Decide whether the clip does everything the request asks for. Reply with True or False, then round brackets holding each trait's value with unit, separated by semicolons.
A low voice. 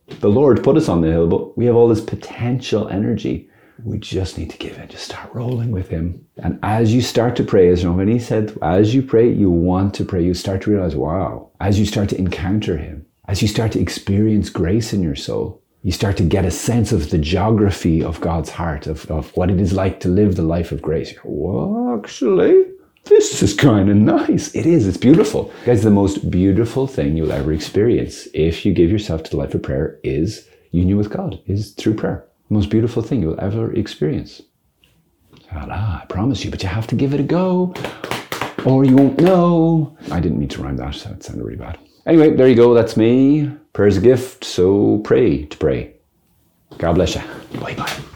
True (105 Hz)